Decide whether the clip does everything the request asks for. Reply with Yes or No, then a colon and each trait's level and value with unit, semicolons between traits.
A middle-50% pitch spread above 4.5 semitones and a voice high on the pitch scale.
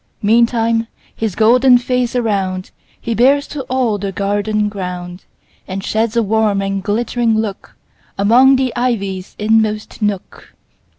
No: average, 3.2 semitones; high, 220 Hz